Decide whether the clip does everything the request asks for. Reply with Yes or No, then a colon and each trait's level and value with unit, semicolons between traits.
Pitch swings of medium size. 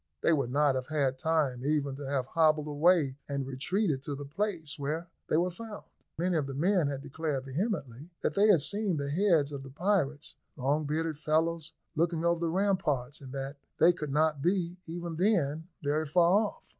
Yes: average, 3.4 semitones